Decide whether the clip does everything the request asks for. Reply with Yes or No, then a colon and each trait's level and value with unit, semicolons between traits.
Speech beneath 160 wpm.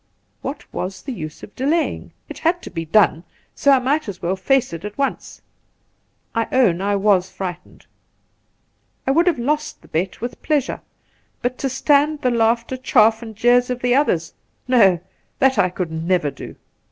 No: average, 180 wpm